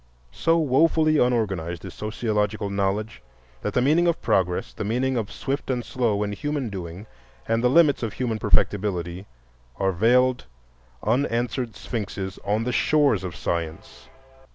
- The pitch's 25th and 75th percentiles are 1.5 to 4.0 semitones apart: No, average, 4.7 semitones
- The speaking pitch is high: No, low, 110 Hz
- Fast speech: No, average, 145 wpm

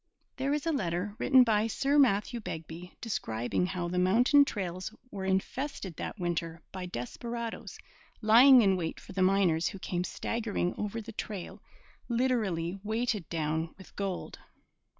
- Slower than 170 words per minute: Yes, average, 150 wpm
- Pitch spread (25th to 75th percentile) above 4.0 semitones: Yes, average, 4.8 semitones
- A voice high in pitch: Yes, high, 195 Hz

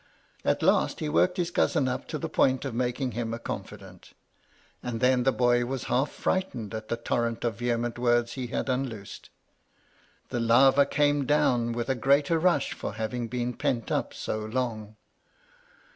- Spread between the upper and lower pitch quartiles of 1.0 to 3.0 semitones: Yes, narrow, 2.5 semitones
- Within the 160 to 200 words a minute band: Yes, average, 175 wpm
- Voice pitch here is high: No, low, 125 Hz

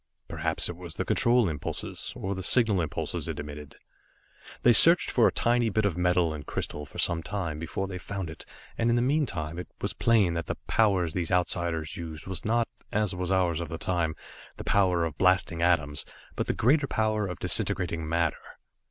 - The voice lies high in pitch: No, very low, 90 Hz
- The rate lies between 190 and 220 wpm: Yes, average, 195 wpm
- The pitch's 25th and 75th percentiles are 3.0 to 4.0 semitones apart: No, average, 4.4 semitones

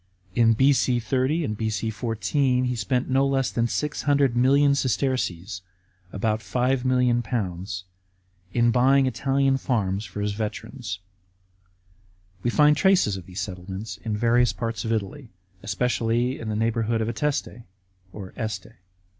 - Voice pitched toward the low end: Yes, low, 120 Hz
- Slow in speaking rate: Yes, slow, 130 wpm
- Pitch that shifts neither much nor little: Yes, average, 3.5 semitones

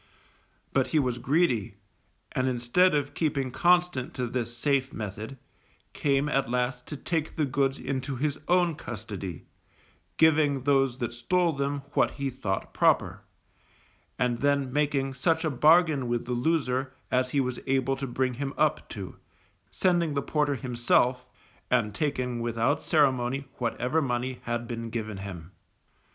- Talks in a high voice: No, low, 130 Hz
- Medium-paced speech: Yes, average, 150 wpm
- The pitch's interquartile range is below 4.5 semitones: Yes, average, 3.2 semitones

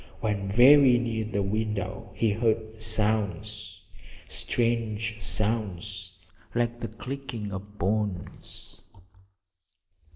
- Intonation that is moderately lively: No, narrow, 2.1 semitones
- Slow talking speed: Yes, slow, 90 wpm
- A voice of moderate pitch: No, low, 110 Hz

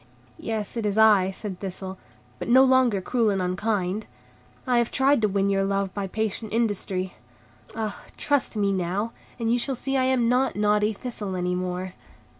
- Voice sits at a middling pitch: No, high, 210 Hz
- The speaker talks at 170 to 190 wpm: Yes, average, 180 wpm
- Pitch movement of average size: Yes, average, 3.6 semitones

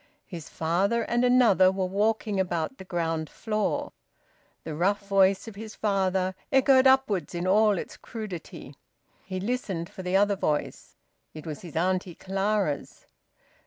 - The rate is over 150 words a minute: No, average, 145 wpm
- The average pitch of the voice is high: Yes, high, 195 Hz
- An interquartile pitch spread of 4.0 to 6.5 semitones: No, average, 3.4 semitones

